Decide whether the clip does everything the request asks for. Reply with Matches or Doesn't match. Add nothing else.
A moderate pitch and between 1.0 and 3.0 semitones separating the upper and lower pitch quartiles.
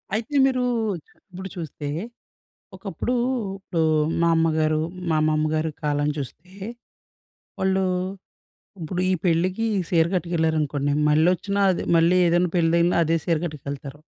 Matches